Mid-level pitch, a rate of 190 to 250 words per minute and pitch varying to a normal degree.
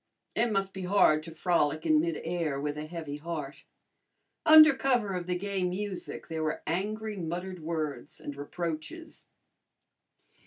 No: medium, 170 Hz; average, 145 wpm; average, 4.1 semitones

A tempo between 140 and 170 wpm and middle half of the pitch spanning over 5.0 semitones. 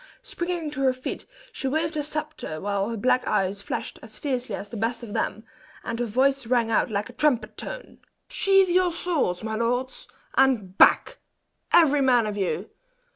No: average, 180 wpm; wide, 5.6 semitones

